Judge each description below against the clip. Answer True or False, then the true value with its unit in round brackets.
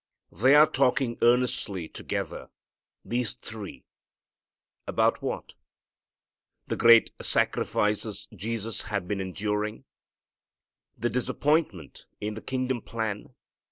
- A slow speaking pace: True (95 wpm)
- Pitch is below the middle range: True (115 Hz)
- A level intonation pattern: False (3.2 semitones)